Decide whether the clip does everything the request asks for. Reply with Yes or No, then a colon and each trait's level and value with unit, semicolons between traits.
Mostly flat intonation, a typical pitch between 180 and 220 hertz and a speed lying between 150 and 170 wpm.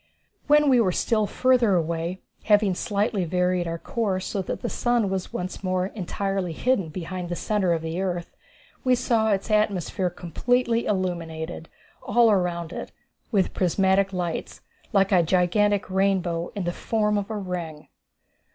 No: average, 3.1 semitones; high, 190 Hz; average, 155 wpm